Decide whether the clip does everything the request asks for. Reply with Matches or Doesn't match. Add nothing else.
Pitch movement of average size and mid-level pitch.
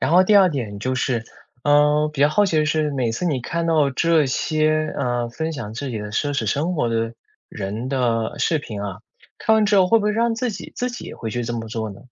Doesn't match